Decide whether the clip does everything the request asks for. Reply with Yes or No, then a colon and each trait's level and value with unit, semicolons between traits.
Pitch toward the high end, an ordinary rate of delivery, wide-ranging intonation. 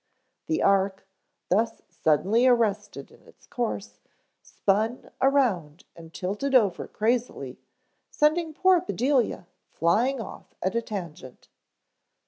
No: high, 215 Hz; slow, 110 wpm; wide, 6.0 semitones